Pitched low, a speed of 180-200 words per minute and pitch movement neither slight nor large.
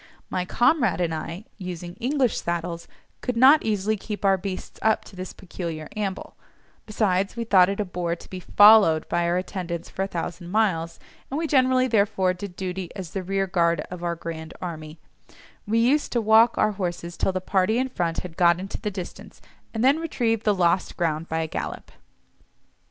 No: medium, 185 Hz; average, 190 wpm; average, 4.1 semitones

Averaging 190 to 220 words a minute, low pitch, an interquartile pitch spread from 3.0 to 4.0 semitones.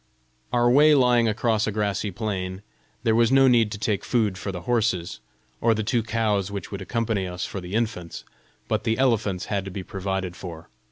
Yes: average, 200 wpm; low, 105 Hz; average, 3.3 semitones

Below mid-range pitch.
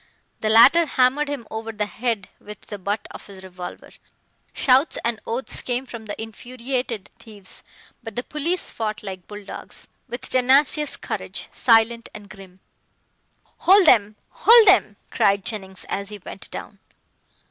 No: high, 225 Hz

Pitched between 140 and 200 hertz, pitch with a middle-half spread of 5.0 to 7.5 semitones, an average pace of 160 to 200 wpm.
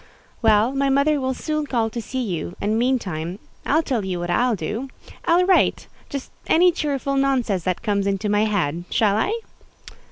No: high, 235 Hz; wide, 5.6 semitones; average, 165 wpm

